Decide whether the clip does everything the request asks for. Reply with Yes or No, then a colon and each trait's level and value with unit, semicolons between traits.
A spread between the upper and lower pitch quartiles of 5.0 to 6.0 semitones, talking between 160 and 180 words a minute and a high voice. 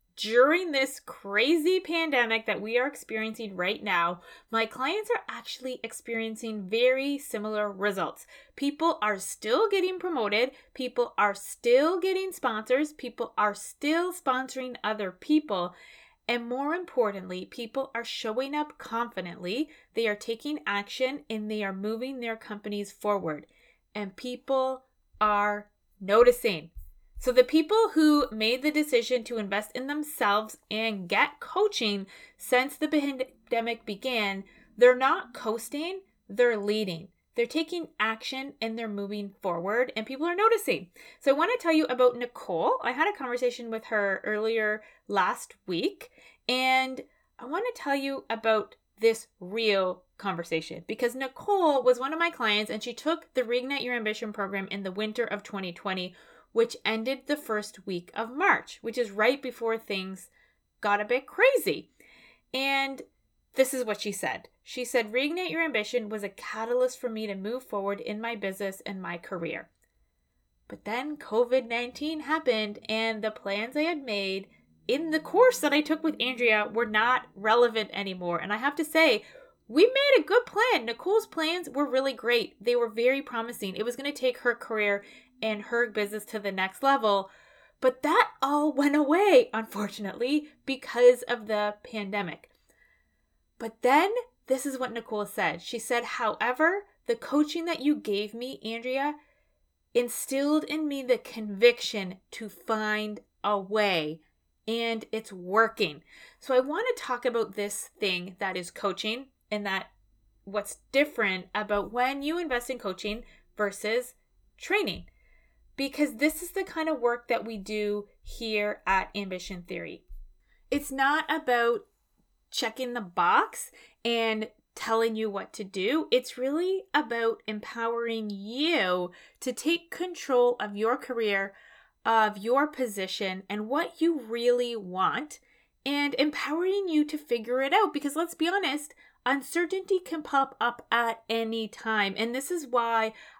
No: average, 5.3 semitones; average, 150 wpm; high, 240 Hz